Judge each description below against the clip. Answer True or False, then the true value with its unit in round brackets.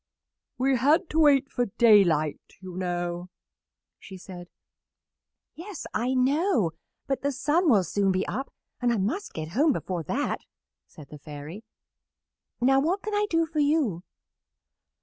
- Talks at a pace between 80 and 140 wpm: False (150 wpm)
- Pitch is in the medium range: False (245 Hz)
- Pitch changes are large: True (8.4 semitones)